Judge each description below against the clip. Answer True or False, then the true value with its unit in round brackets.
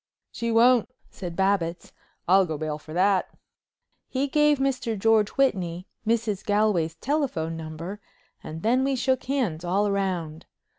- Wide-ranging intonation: True (6.3 semitones)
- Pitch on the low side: False (200 Hz)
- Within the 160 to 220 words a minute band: False (140 wpm)